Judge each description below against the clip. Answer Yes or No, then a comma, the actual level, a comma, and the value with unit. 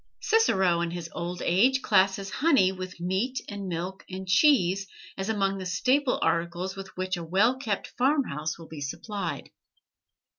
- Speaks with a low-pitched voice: No, high, 190 Hz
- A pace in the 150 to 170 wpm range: Yes, average, 160 wpm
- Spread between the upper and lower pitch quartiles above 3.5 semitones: Yes, average, 4.0 semitones